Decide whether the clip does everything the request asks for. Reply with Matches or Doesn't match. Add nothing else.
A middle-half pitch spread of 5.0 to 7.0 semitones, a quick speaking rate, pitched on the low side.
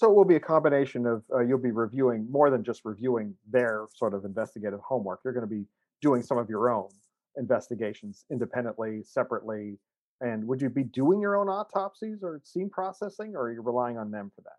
Matches